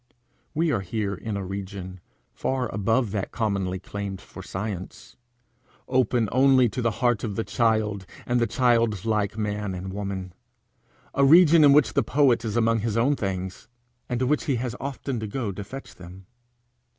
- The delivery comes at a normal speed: Yes, average, 175 wpm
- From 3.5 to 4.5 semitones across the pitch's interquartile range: Yes, average, 4.2 semitones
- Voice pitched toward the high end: No, low, 110 Hz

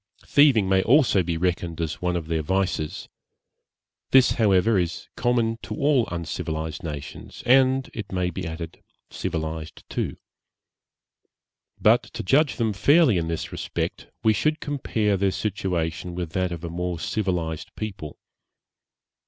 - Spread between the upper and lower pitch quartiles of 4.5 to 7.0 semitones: Yes, wide, 5.4 semitones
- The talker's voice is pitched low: Yes, very low, 95 Hz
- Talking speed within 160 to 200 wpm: No, average, 140 wpm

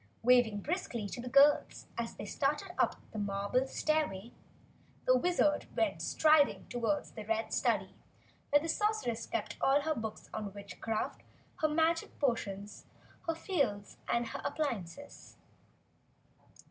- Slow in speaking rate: Yes, slow, 130 wpm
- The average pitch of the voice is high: Yes, very high, 250 Hz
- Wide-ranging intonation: Yes, wide, 6.0 semitones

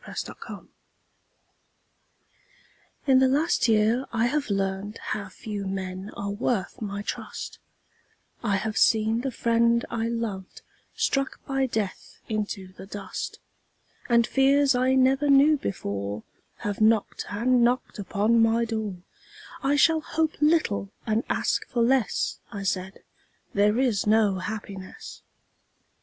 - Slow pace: Yes, slow, 130 wpm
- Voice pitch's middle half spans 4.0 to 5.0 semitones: Yes, average, 4.3 semitones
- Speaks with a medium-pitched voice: No, high, 225 Hz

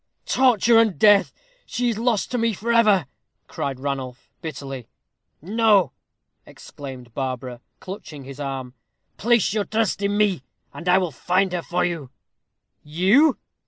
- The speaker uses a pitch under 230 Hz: Yes, medium, 185 Hz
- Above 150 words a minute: No, average, 140 wpm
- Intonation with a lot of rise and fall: Yes, wide, 7.9 semitones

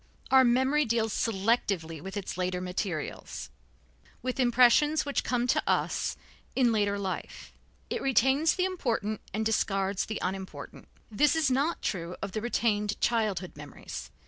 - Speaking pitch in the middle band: No, high, 220 Hz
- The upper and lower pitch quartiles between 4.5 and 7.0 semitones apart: Yes, average, 5.0 semitones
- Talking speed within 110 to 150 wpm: Yes, average, 145 wpm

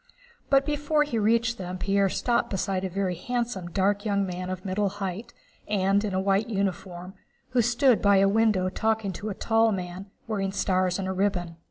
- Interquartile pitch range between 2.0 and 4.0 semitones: Yes, average, 3.1 semitones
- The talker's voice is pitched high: Yes, high, 200 Hz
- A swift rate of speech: No, average, 185 wpm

